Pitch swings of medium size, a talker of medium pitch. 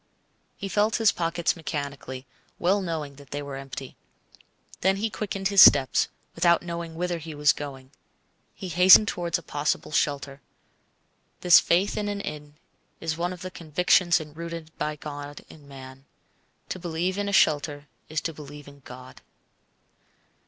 Yes: average, 3.7 semitones; medium, 160 Hz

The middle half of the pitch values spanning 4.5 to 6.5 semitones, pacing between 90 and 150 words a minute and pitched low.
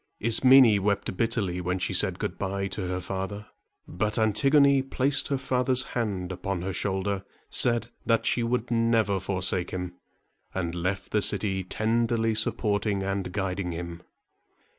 No: average, 3.6 semitones; average, 145 wpm; low, 100 Hz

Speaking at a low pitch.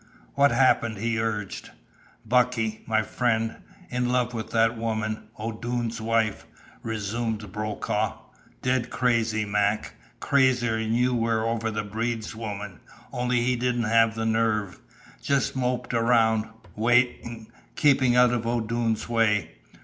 Yes: low, 115 Hz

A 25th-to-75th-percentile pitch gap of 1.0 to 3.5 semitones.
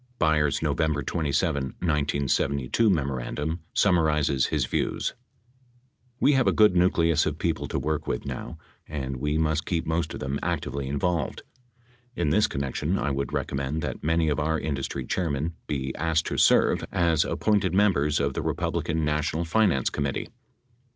Yes: average, 2.9 semitones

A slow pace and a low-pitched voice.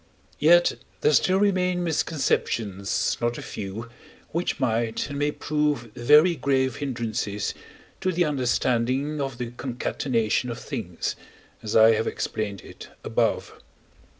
Yes: slow, 125 wpm; low, 125 Hz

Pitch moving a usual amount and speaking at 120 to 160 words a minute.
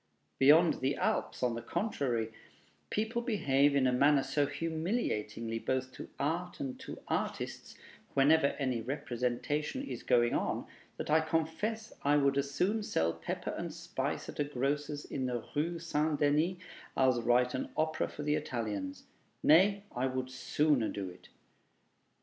Yes: average, 4.1 semitones; average, 155 wpm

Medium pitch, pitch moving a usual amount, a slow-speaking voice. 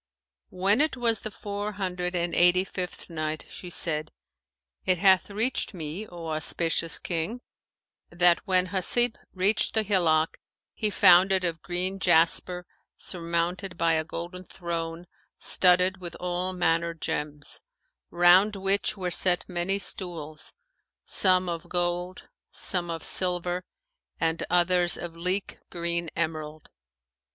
No: medium, 180 Hz; narrow, 2.0 semitones; slow, 130 wpm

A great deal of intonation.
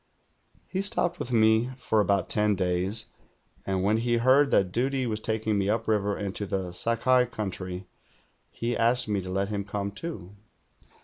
No: average, 3.2 semitones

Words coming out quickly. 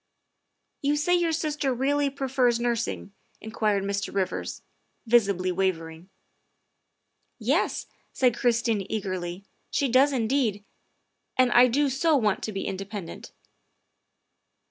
No: average, 145 wpm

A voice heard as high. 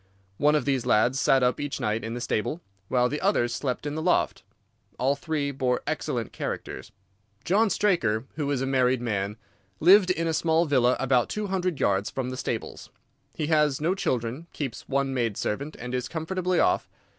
No: low, 135 Hz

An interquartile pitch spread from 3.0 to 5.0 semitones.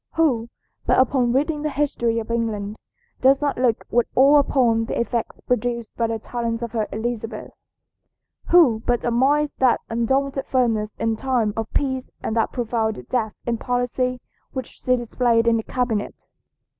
No: narrow, 2.5 semitones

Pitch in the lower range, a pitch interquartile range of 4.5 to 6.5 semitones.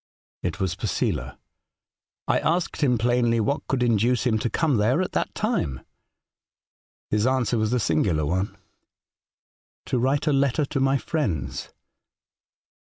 Yes: low, 120 Hz; wide, 5.4 semitones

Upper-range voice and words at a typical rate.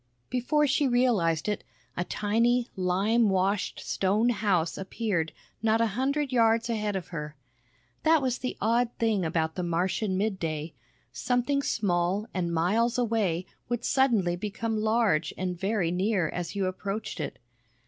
Yes: high, 210 Hz; average, 145 wpm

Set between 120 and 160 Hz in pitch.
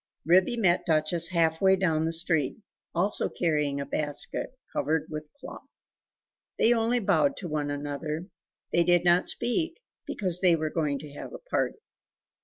No: medium, 170 Hz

